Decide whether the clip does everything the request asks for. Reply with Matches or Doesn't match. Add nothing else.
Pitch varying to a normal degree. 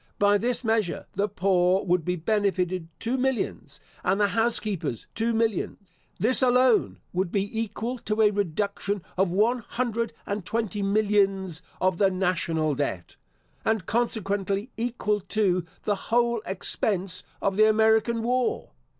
Matches